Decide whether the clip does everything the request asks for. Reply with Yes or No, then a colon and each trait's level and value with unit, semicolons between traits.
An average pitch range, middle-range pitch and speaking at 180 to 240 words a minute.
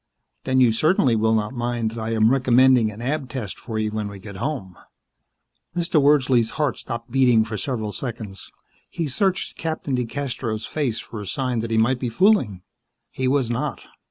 No: average, 3.3 semitones; low, 120 Hz; average, 185 wpm